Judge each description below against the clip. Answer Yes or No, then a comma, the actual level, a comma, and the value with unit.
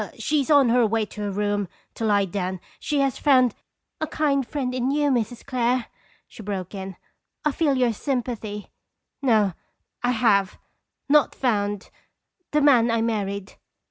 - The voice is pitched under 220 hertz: No, high, 235 Hz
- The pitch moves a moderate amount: Yes, average, 4.8 semitones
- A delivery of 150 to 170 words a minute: Yes, average, 160 wpm